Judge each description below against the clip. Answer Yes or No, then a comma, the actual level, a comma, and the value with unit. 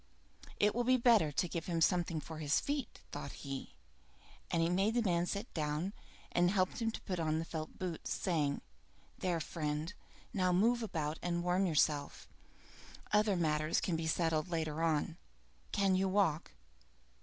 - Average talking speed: Yes, average, 165 wpm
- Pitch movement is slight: No, average, 3.6 semitones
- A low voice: No, medium, 170 Hz